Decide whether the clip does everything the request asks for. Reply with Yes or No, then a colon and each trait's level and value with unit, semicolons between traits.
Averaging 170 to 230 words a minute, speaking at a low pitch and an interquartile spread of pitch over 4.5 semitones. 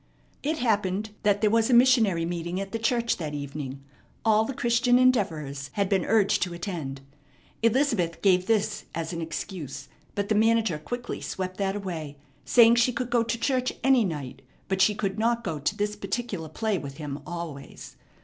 No: average, 180 wpm; high, 200 Hz; wide, 5.5 semitones